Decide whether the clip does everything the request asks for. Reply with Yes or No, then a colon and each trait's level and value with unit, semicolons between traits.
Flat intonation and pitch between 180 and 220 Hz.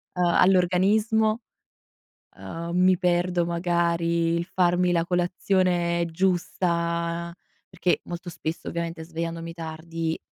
No: narrow, 1.3 semitones; medium, 170 Hz